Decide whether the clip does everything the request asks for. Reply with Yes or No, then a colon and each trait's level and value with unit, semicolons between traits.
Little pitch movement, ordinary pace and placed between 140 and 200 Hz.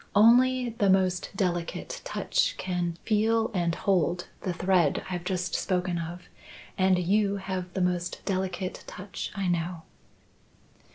No: narrow, 2.2 semitones; slow, 130 wpm; medium, 185 Hz